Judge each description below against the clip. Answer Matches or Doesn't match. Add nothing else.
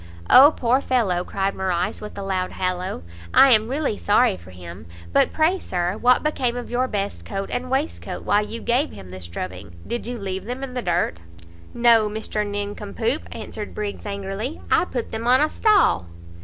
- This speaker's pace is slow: Doesn't match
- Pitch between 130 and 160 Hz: Doesn't match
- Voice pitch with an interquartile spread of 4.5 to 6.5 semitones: Matches